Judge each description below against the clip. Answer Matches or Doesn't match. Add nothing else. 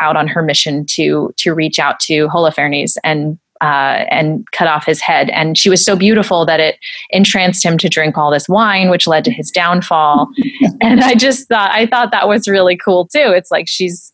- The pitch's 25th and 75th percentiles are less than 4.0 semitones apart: Doesn't match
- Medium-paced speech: Doesn't match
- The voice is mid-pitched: Matches